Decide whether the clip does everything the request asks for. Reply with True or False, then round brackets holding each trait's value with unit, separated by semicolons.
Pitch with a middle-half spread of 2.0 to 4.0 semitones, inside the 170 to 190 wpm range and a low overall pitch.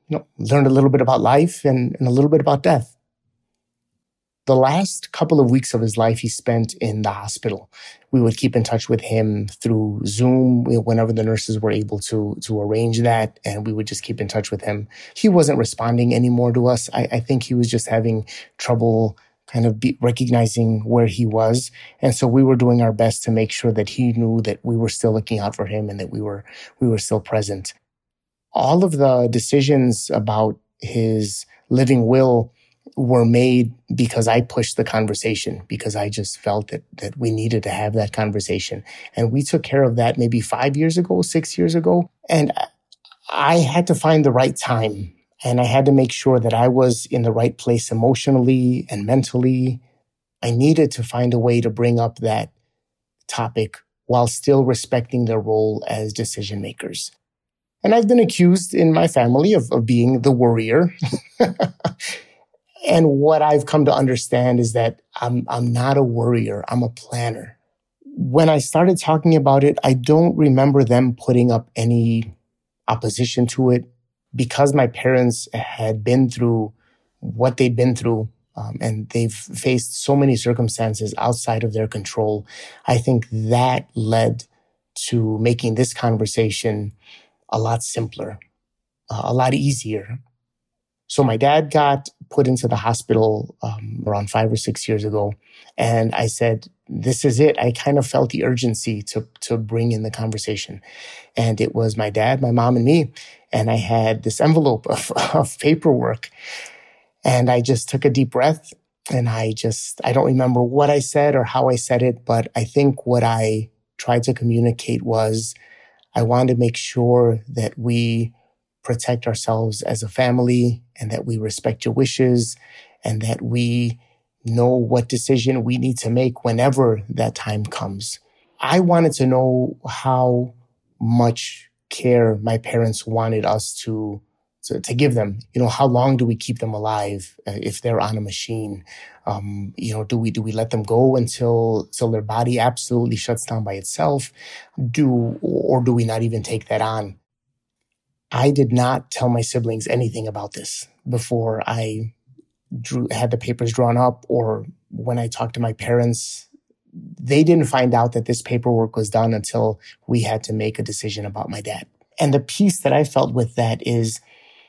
True (2.5 semitones; 180 wpm; 120 Hz)